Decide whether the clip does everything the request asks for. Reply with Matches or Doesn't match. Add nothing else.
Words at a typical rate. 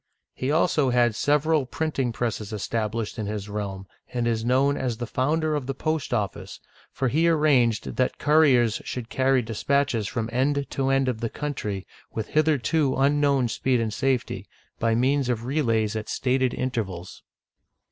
Matches